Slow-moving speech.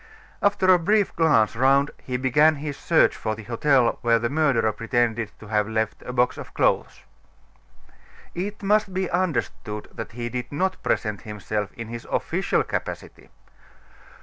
No: average, 155 wpm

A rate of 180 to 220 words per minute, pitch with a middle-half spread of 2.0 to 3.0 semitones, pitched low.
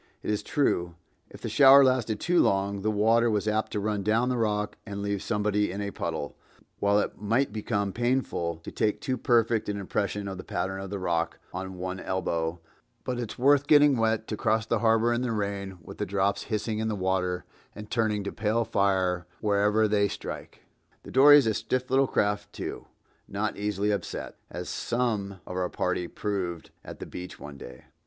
Yes: average, 200 wpm; average, 2.7 semitones; low, 105 Hz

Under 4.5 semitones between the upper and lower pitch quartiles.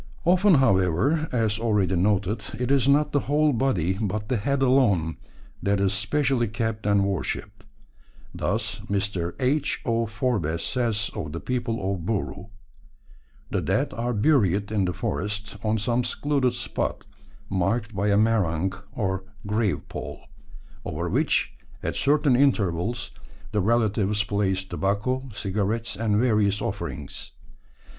Yes: average, 4.1 semitones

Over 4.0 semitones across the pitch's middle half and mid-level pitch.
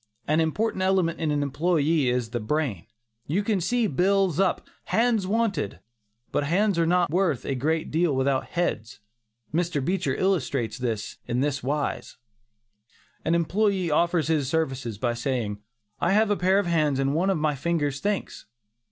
Yes: wide, 5.5 semitones; medium, 160 Hz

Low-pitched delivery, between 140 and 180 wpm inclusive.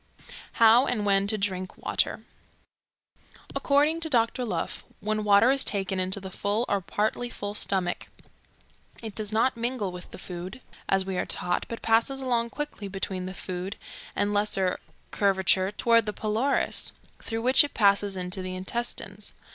No: high, 205 Hz; average, 160 wpm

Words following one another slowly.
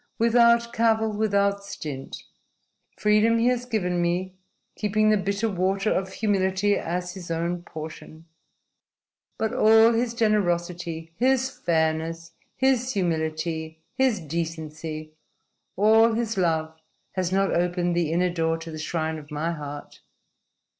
Yes: slow, 125 wpm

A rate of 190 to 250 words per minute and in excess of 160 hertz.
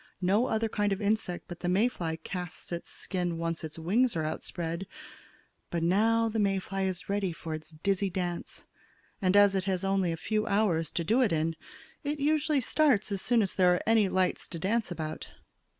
Yes: average, 200 wpm; high, 190 Hz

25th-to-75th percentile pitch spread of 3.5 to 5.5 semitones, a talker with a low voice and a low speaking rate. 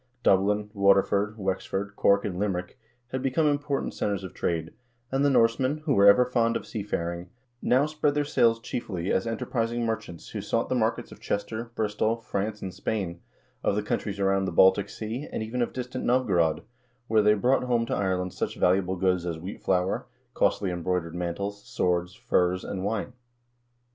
No: average, 3.9 semitones; low, 100 Hz; average, 175 wpm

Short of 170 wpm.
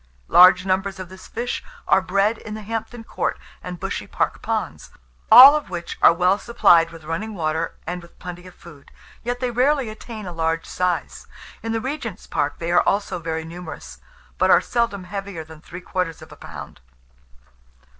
No: average, 185 wpm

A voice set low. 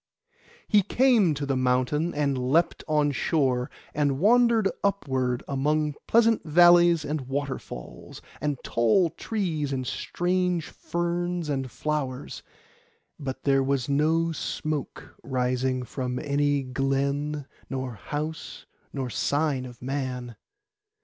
No: medium, 145 Hz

